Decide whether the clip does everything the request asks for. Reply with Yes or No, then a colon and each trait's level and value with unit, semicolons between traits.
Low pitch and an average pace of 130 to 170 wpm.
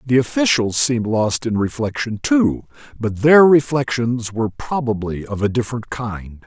Yes: low, 120 Hz; average, 150 wpm